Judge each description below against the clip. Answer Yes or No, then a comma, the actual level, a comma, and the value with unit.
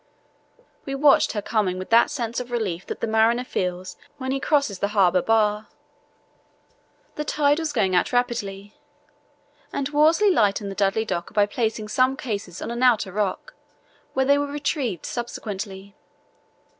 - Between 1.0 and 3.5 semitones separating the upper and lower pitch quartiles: No, average, 4.9 semitones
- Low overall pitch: No, high, 225 Hz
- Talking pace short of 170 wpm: Yes, average, 155 wpm